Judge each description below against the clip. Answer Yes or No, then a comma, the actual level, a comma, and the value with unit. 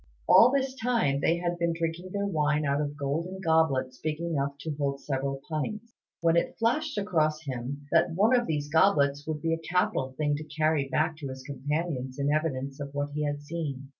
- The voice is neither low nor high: Yes, medium, 155 Hz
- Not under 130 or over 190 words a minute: No, average, 200 wpm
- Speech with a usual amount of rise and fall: Yes, average, 3.2 semitones